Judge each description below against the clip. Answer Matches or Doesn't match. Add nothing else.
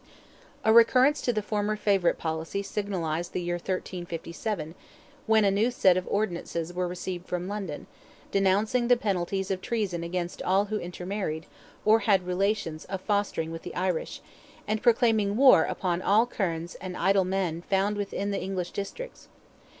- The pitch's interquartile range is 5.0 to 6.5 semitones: Doesn't match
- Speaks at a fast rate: Doesn't match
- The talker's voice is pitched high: Matches